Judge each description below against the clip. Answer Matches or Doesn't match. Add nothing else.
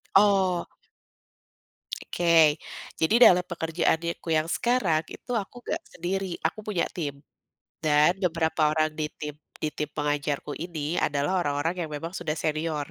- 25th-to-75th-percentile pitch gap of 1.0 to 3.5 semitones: Matches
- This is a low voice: Doesn't match